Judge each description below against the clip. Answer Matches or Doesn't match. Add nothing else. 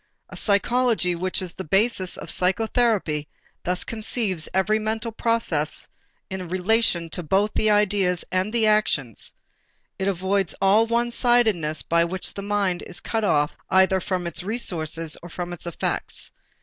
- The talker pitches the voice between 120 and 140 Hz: Doesn't match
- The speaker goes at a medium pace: Matches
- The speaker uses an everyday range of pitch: Matches